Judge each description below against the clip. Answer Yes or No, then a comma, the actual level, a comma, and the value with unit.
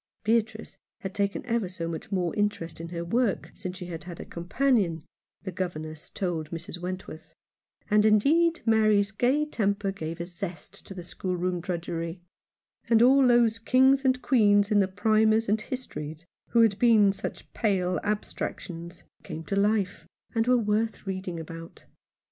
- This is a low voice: No, high, 200 Hz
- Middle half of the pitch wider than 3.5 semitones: Yes, average, 4.2 semitones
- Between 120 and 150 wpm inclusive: No, average, 160 wpm